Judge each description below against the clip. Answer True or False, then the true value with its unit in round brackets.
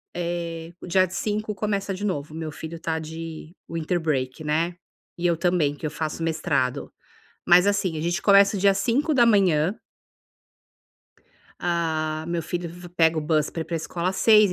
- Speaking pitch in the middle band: True (170 Hz)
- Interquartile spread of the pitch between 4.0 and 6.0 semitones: False (3.0 semitones)